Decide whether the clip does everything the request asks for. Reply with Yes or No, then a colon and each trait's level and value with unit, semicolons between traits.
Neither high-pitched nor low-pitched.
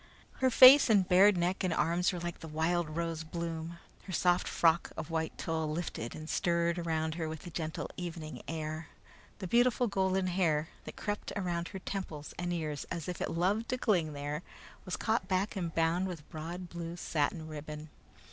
Yes: medium, 170 Hz